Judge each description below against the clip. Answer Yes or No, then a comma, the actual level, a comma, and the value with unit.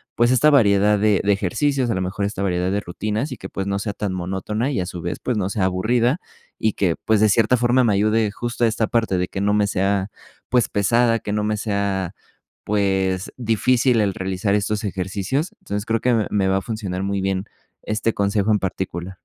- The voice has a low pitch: Yes, low, 105 Hz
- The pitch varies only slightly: No, average, 3.0 semitones